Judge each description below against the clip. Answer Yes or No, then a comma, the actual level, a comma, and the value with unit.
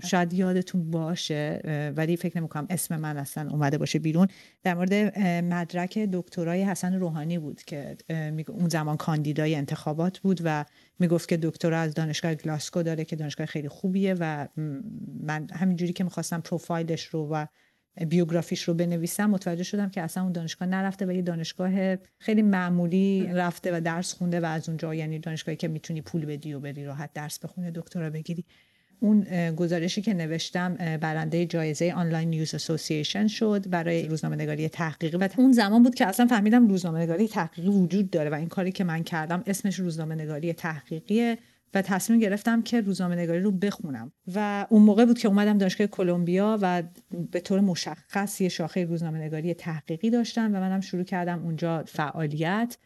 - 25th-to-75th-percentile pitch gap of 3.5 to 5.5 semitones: No, average, 3.0 semitones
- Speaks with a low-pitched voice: No, medium, 175 Hz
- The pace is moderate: No, fast, 170 wpm